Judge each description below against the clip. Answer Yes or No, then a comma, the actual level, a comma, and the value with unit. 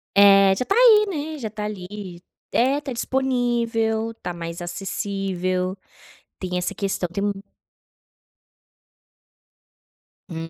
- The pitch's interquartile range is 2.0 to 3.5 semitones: No, average, 4.7 semitones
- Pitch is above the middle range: Yes, high, 200 Hz